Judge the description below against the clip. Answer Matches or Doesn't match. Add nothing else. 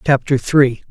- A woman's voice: Doesn't match